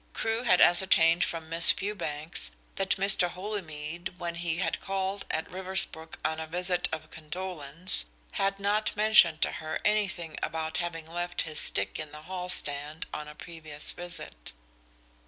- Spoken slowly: No, average, 155 wpm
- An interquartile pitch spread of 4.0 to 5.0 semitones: No, average, 3.2 semitones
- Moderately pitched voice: Yes, medium, 170 Hz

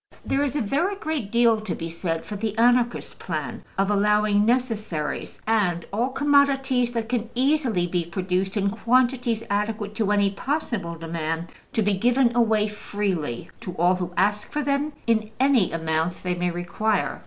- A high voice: Yes, high, 210 Hz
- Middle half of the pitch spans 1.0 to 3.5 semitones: No, average, 5.1 semitones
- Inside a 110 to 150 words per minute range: No, average, 165 wpm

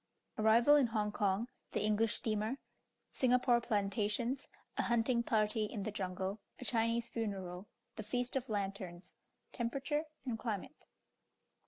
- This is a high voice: Yes, high, 220 Hz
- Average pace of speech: No, slow, 130 wpm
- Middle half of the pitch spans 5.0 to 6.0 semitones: No, average, 2.7 semitones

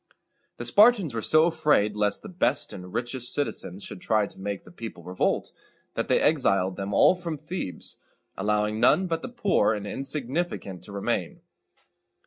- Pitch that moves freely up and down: Yes, wide, 8.0 semitones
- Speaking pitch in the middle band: No, low, 115 Hz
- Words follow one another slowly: No, average, 165 wpm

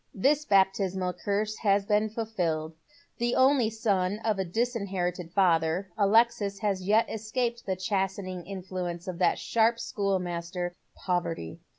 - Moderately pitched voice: No, high, 195 Hz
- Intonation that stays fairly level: No, average, 3.4 semitones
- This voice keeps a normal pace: No, slow, 125 wpm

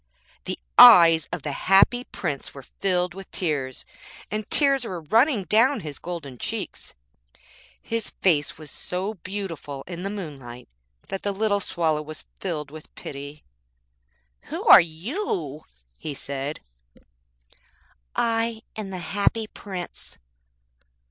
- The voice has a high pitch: No, medium, 180 Hz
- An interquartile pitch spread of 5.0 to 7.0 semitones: Yes, average, 5.3 semitones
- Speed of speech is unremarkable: No, slow, 125 wpm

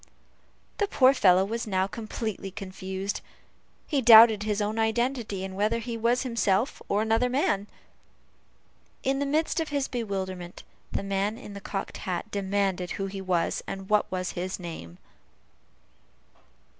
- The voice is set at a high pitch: Yes, high, 205 Hz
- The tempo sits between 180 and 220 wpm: No, average, 145 wpm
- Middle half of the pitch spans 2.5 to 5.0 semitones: Yes, average, 3.5 semitones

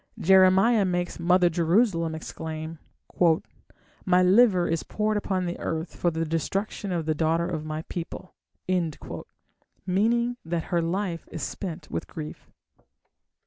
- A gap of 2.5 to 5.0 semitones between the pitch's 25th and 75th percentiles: Yes, average, 2.8 semitones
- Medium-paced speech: No, slow, 130 wpm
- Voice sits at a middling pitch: Yes, medium, 175 Hz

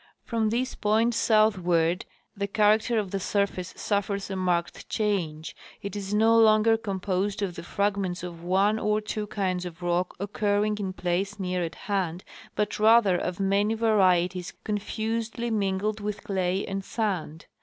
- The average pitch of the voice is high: Yes, high, 200 Hz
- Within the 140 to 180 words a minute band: Yes, average, 155 wpm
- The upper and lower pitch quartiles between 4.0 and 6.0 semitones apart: No, average, 2.8 semitones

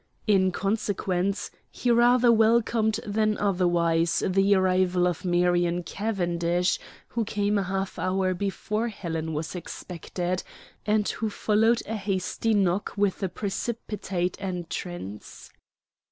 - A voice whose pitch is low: No, high, 190 Hz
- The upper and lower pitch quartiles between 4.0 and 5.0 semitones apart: No, average, 3.2 semitones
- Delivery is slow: Yes, slow, 115 wpm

